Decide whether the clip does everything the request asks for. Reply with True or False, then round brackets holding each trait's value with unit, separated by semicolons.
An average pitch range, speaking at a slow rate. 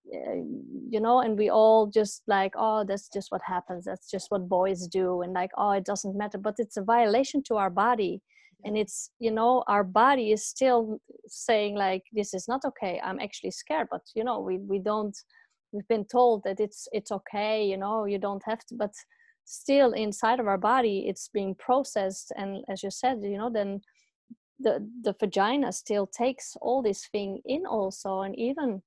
False (3.3 semitones; 195 wpm)